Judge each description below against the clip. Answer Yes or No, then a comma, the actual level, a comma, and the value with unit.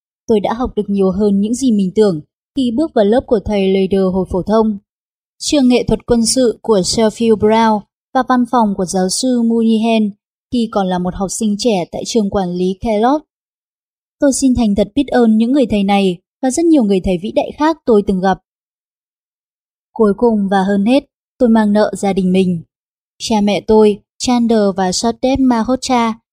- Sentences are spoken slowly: No, average, 195 wpm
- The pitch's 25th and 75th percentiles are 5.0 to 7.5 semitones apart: No, average, 3.5 semitones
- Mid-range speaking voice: No, high, 220 Hz